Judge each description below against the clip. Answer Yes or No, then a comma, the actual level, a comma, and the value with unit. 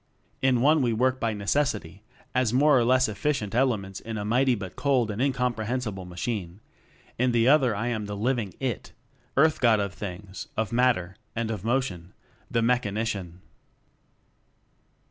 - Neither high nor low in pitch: No, low, 115 Hz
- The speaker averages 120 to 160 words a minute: Yes, average, 155 wpm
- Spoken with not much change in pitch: No, average, 4.0 semitones